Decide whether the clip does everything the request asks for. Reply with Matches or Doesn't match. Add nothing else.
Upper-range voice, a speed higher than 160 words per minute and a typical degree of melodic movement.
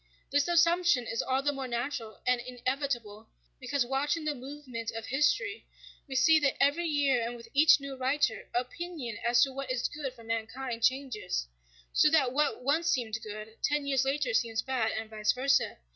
Matches